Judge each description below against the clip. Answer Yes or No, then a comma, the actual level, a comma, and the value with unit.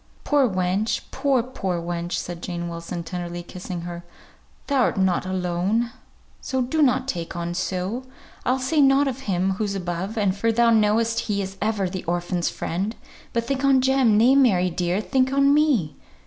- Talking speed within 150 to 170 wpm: Yes, average, 165 wpm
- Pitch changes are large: Yes, wide, 6.5 semitones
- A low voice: No, high, 200 Hz